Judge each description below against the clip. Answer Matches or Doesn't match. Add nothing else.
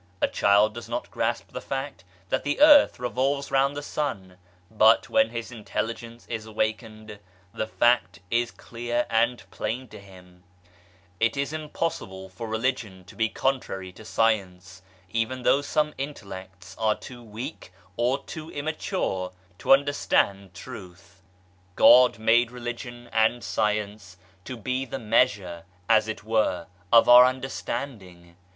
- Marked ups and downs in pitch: Doesn't match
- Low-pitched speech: Matches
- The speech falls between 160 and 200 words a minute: Doesn't match